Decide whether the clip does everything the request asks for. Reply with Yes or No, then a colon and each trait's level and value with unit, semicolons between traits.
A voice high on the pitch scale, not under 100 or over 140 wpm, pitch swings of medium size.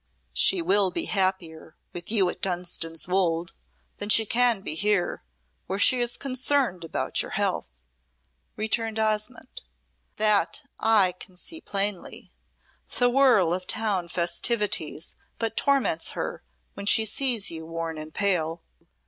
Yes: high, 195 Hz; slow, 135 wpm; average, 4.5 semitones